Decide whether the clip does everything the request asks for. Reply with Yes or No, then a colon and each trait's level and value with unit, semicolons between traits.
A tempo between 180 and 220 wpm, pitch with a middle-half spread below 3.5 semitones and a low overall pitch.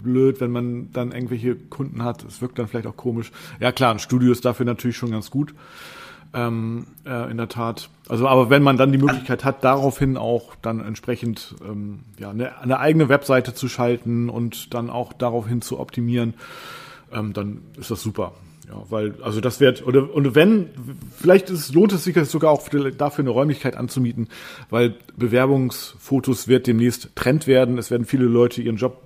Yes: average, 185 wpm; narrow, 2.5 semitones; low, 125 Hz